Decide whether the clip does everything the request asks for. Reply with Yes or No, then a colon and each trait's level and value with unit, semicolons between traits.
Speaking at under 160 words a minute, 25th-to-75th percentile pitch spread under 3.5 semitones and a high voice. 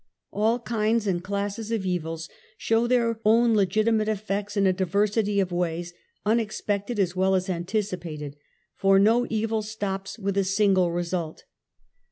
Yes: average, 150 wpm; average, 2.9 semitones; high, 200 Hz